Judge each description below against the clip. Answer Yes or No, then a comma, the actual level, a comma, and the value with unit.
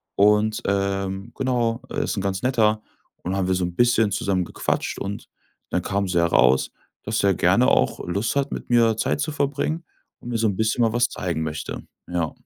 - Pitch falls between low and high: No, low, 105 Hz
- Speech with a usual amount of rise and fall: Yes, average, 4.0 semitones